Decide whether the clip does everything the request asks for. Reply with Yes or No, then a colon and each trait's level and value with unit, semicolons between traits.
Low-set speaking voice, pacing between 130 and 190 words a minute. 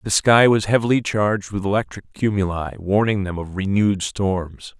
Yes: low, 100 Hz; average, 165 wpm